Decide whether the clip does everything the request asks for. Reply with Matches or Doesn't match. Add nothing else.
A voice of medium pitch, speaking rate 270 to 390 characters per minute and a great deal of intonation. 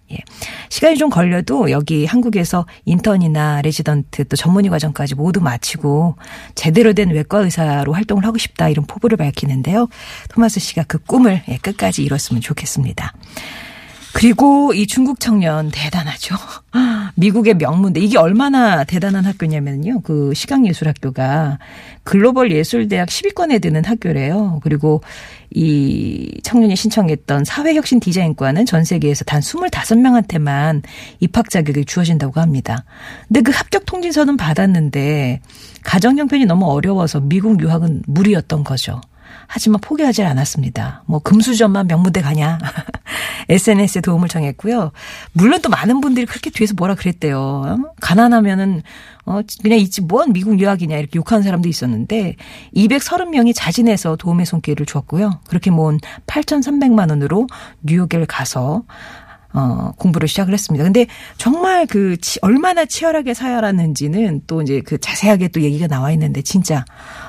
Matches